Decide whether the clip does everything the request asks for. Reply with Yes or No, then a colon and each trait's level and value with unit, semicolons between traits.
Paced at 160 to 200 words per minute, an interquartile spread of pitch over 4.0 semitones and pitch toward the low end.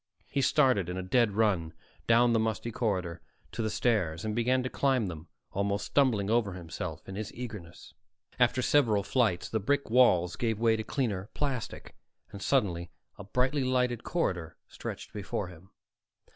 Yes: average, 165 wpm; average, 5.1 semitones; low, 110 Hz